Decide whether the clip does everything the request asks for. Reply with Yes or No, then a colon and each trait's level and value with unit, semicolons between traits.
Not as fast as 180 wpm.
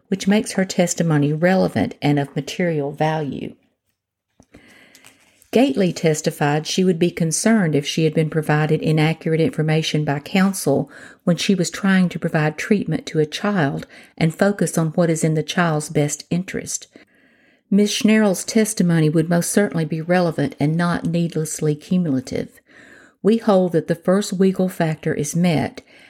Yes: average, 150 wpm